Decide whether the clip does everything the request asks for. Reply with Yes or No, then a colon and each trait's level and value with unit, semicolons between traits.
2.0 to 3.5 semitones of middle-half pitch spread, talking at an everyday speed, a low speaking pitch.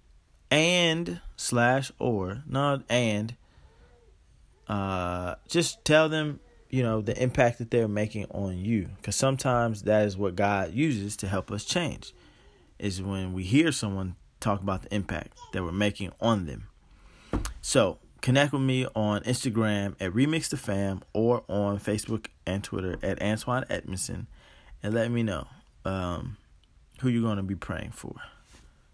No: average, 4.4 semitones; average, 150 wpm; low, 105 Hz